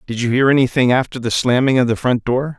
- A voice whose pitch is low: Yes, low, 125 Hz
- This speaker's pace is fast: Yes, fast, 255 wpm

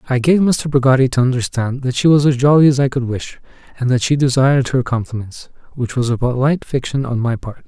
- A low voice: Yes, low, 130 Hz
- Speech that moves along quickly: Yes, fast, 220 wpm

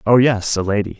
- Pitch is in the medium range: No, low, 110 Hz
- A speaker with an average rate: Yes, average, 180 wpm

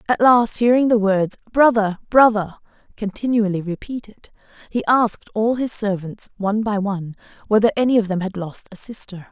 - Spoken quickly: No, average, 160 wpm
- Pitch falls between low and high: No, high, 215 Hz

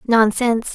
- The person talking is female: Yes, female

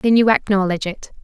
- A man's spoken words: No, female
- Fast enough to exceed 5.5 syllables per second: Yes, 6.4 syllables/s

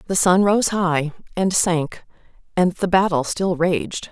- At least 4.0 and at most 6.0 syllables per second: No, 3.8 syllables/s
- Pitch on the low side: No, medium, 175 Hz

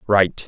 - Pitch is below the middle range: Yes, very low, 95 Hz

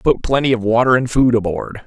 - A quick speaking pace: Yes, fast, 225 wpm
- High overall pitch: No, low, 120 Hz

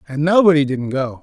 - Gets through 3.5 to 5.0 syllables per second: No, 5.6 syllables/s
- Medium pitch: Yes, medium, 150 Hz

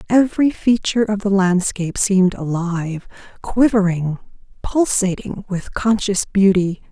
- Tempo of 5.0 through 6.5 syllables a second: No, 4.6 syllables/s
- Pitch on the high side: Yes, high, 195 Hz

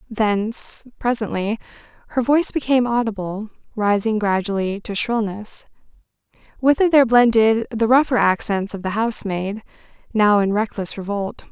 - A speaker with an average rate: No, slow, 125 wpm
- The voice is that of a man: No, female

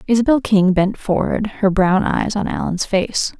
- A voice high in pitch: Yes, high, 205 Hz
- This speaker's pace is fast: No, average, 175 wpm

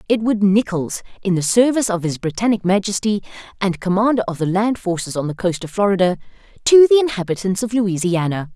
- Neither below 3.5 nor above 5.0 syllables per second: No, 6.0 syllables/s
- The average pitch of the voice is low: No, high, 200 Hz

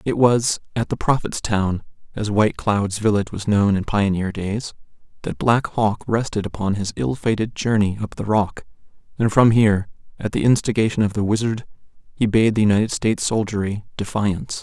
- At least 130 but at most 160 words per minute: No, average, 175 wpm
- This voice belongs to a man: Yes, male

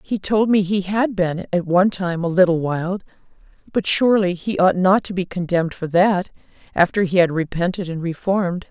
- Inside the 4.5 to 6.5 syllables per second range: Yes, 5.2 syllables/s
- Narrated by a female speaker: Yes, female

